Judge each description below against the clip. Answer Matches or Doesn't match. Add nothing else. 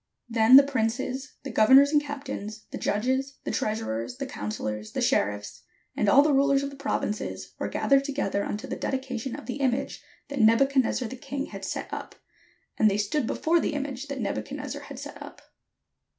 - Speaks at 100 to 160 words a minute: Doesn't match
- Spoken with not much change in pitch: Doesn't match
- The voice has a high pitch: Matches